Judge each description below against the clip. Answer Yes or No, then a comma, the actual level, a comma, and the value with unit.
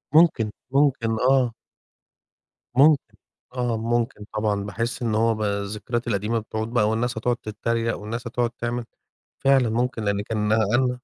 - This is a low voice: Yes, low, 115 Hz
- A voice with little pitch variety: Yes, narrow, 2.2 semitones